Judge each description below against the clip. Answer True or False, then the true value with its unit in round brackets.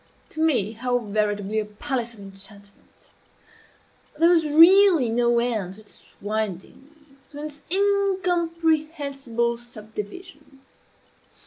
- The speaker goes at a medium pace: False (105 wpm)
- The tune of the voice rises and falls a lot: True (6.8 semitones)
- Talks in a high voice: True (250 Hz)